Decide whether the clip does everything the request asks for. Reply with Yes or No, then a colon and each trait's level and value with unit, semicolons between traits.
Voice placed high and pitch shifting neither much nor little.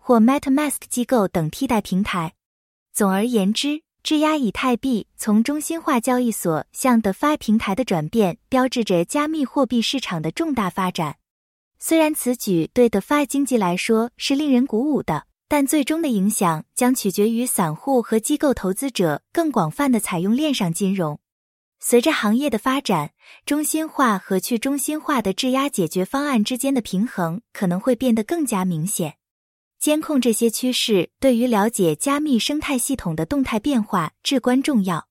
No: high, 240 Hz; wide, 6.1 semitones